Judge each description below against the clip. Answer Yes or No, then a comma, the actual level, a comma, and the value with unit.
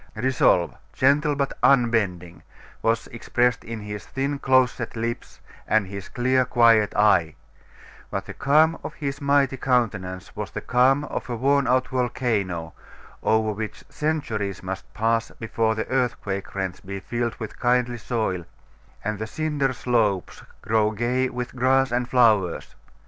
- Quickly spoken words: No, average, 145 wpm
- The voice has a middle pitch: No, low, 120 Hz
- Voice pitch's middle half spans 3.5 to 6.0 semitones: Yes, average, 3.8 semitones